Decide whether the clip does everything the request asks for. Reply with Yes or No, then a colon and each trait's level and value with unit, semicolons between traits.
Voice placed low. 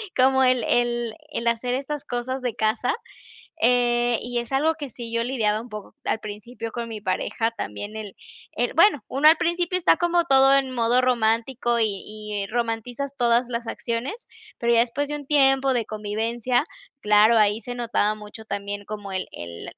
No: high, 240 Hz